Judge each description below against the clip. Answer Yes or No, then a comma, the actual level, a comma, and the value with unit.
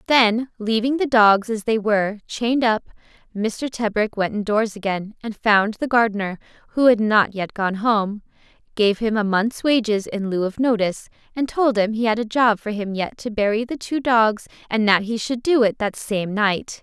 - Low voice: No, high, 220 Hz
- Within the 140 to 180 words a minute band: No, average, 200 wpm